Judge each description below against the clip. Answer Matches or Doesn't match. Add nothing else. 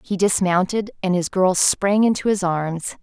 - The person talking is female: Matches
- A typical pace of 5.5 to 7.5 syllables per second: Doesn't match